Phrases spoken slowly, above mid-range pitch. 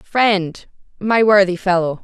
Yes: slow, 120 wpm; high, 195 Hz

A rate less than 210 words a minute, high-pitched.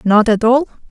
Yes: average, 200 wpm; high, 235 Hz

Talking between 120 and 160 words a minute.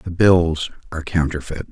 Yes: average, 140 wpm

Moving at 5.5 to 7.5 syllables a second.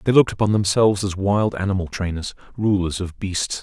Yes: 5.8 syllables/s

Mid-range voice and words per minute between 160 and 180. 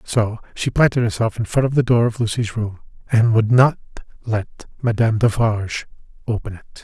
No: low, 115 Hz; average, 175 wpm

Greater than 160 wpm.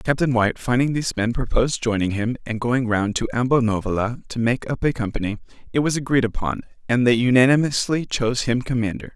Yes: average, 185 wpm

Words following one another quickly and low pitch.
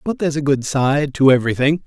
No: fast, 225 wpm; medium, 145 Hz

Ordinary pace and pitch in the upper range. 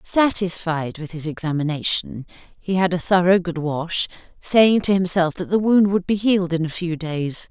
No: average, 185 wpm; medium, 175 Hz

